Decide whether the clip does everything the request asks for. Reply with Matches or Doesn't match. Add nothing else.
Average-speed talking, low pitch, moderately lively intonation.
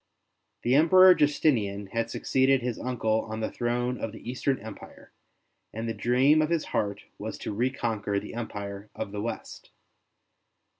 Matches